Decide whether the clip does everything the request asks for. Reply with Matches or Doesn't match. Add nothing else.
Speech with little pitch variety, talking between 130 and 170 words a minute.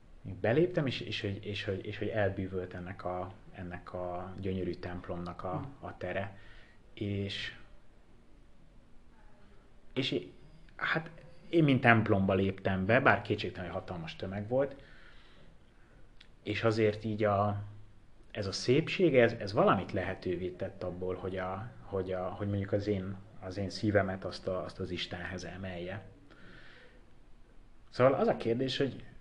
Doesn't match